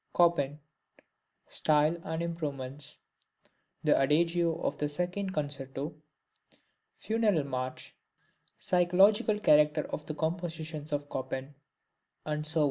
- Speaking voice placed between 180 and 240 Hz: No, medium, 155 Hz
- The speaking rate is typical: No, slow, 95 wpm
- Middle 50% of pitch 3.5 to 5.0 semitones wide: No, average, 2.9 semitones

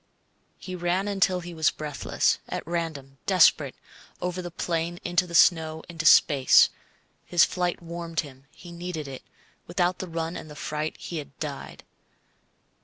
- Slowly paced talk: No, average, 155 wpm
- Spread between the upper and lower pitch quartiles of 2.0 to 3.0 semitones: Yes, narrow, 2.4 semitones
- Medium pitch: Yes, medium, 170 Hz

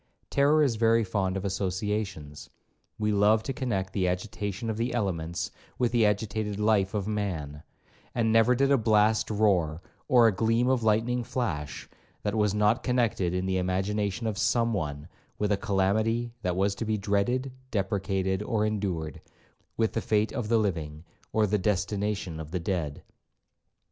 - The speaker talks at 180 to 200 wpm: No, average, 165 wpm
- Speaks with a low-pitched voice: Yes, low, 105 Hz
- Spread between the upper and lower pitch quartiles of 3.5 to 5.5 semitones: No, average, 3.1 semitones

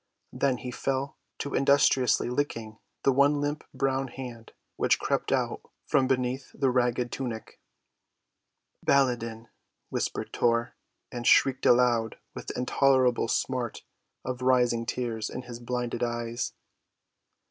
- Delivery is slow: Yes, slow, 125 wpm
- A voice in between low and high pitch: No, low, 125 Hz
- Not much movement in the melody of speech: Yes, narrow, 2.2 semitones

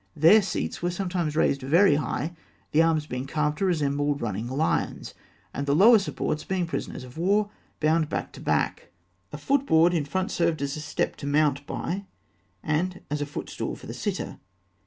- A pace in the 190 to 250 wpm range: Yes, average, 200 wpm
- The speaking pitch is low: No, medium, 155 Hz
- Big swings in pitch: No, average, 3.8 semitones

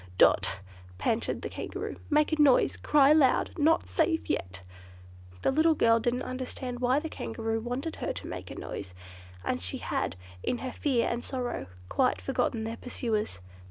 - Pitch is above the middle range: Yes, very high, 250 Hz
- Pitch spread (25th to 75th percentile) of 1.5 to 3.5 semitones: No, average, 4.3 semitones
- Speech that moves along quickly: No, average, 165 wpm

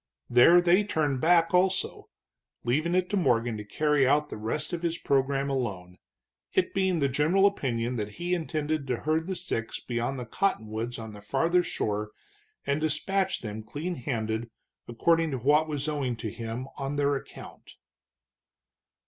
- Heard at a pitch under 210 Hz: Yes, medium, 140 Hz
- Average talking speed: Yes, average, 165 wpm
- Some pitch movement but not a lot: No, wide, 6.0 semitones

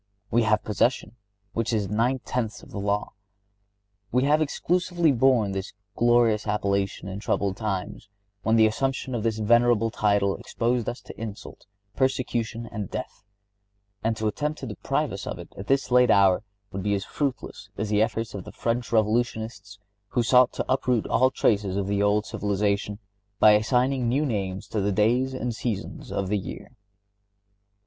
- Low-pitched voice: Yes, low, 110 Hz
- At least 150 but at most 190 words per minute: Yes, average, 170 wpm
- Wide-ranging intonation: No, average, 3.2 semitones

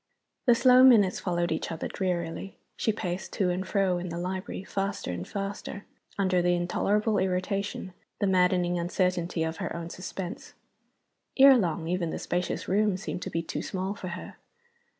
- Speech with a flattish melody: Yes, narrow, 2.2 semitones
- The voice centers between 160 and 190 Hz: Yes, medium, 185 Hz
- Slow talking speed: No, average, 170 wpm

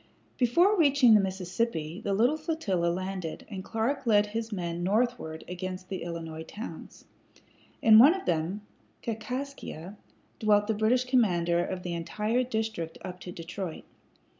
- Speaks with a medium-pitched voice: No, high, 205 Hz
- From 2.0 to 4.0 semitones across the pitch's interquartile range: No, average, 5.1 semitones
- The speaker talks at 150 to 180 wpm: No, average, 140 wpm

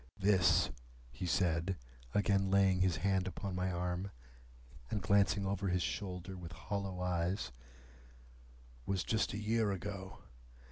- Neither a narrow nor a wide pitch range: No, narrow, 1.7 semitones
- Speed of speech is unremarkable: No, slow, 130 wpm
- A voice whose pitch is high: No, very low, 95 Hz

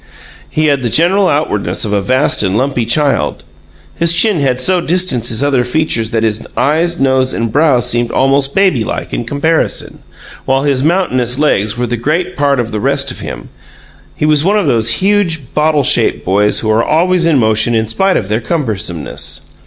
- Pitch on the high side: No, low, 135 Hz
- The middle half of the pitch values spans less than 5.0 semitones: No, wide, 5.5 semitones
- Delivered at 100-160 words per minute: No, average, 190 wpm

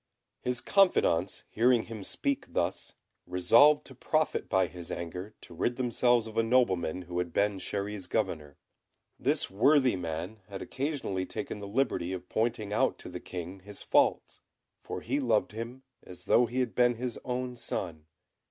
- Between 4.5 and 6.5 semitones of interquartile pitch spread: Yes, average, 5.3 semitones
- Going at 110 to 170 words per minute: Yes, average, 165 wpm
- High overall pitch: No, low, 110 Hz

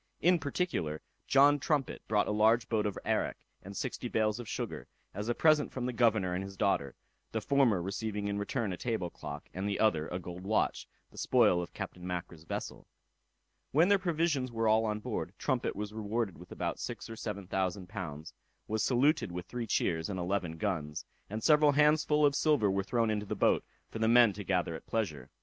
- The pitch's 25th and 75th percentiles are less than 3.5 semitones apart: No, average, 4.7 semitones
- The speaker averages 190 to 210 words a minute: Yes, fast, 205 wpm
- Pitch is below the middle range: Yes, low, 105 Hz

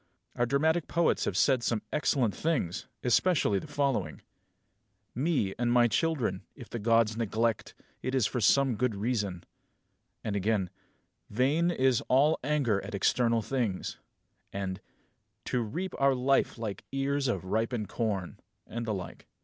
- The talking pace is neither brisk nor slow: Yes, average, 145 wpm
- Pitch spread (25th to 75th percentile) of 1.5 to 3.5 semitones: No, average, 4.6 semitones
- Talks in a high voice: No, low, 120 Hz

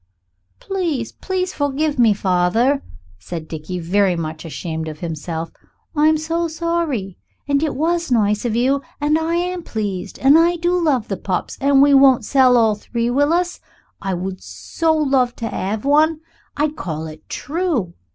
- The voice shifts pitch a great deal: Yes, wide, 8.6 semitones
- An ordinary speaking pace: Yes, average, 170 wpm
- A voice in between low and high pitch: No, very high, 265 Hz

